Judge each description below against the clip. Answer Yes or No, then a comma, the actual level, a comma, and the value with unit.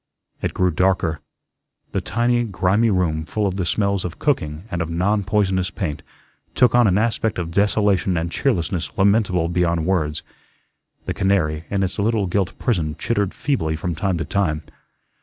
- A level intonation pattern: No, average, 3.5 semitones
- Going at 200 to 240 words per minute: No, average, 165 wpm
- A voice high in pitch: No, very low, 95 Hz